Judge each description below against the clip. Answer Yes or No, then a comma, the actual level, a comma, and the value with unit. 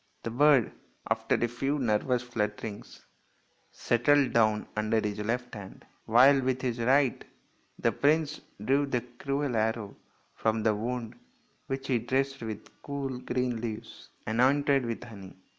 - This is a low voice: Yes, low, 120 Hz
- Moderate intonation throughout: Yes, average, 3.4 semitones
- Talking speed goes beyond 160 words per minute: No, average, 140 wpm